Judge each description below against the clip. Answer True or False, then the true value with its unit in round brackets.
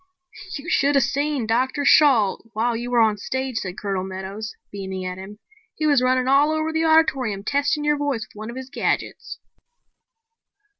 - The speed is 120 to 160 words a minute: False (180 wpm)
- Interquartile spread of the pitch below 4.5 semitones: False (5.5 semitones)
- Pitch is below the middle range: False (255 Hz)